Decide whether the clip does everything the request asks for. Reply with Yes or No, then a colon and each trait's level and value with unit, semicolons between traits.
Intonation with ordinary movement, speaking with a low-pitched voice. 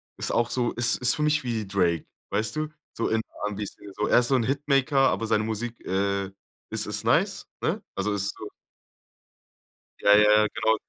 Yes: average, 3.4 semitones; low, 110 Hz